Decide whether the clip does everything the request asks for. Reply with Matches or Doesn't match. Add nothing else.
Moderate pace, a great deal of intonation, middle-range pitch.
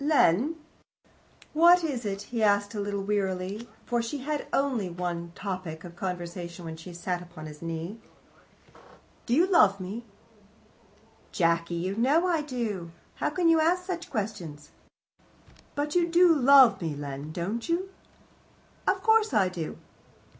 Doesn't match